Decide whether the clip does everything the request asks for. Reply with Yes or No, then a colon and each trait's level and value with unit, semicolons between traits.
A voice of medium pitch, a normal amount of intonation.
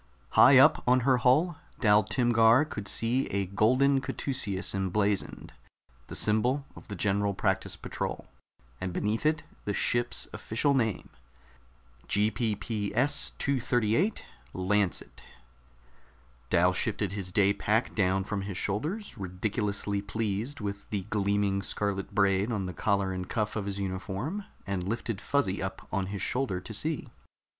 No: low, 105 Hz; average, 3.8 semitones